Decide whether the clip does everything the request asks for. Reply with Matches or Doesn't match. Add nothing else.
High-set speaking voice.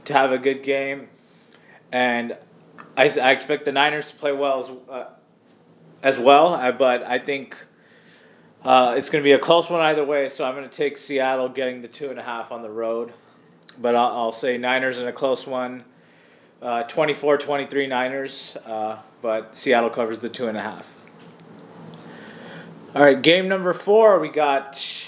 Doesn't match